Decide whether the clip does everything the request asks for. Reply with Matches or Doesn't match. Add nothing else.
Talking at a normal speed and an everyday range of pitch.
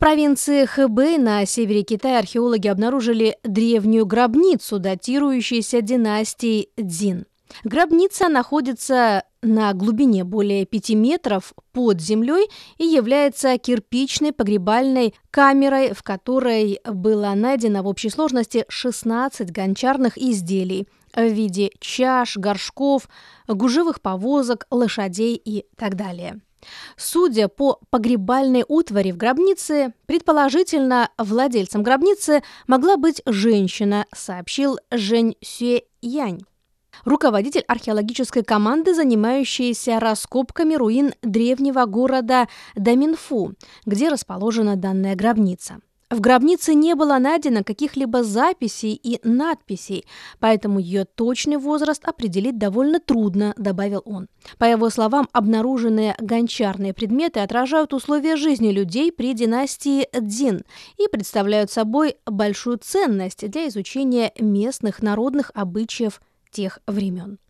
Doesn't match